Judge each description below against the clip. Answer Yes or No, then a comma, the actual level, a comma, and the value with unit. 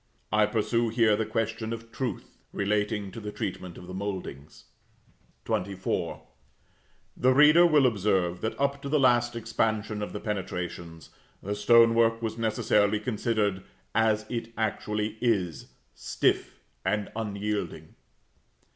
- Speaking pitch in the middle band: No, low, 110 Hz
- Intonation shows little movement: Yes, narrow, 2.3 semitones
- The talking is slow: Yes, slow, 130 wpm